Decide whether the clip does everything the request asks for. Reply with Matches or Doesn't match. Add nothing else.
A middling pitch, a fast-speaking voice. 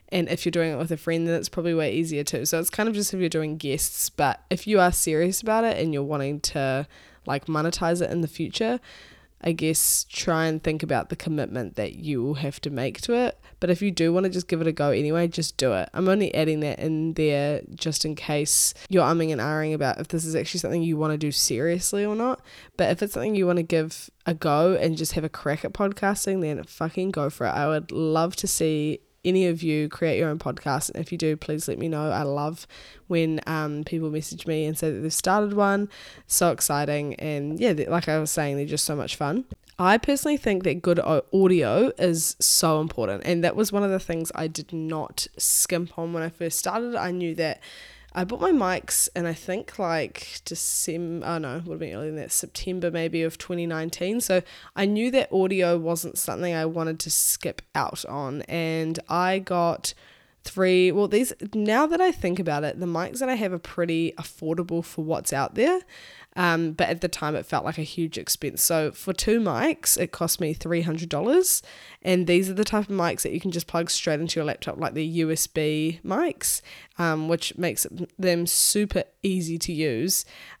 Matches